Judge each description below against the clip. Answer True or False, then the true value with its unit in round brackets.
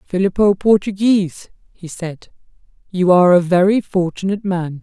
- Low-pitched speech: False (185 Hz)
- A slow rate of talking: True (125 wpm)